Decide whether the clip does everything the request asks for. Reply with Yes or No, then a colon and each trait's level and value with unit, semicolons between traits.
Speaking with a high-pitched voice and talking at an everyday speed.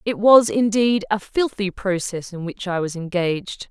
Yes: high, 200 Hz; average, 180 wpm